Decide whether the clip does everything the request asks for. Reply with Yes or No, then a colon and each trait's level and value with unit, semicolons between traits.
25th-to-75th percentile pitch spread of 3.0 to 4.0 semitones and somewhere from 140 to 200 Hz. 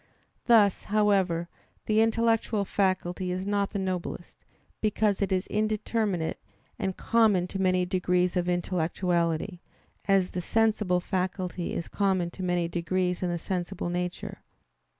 No: narrow, 2.4 semitones; medium, 185 Hz